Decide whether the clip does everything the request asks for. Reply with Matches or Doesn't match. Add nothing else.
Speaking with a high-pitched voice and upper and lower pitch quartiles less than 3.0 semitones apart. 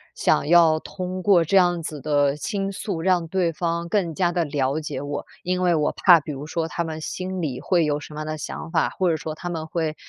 Doesn't match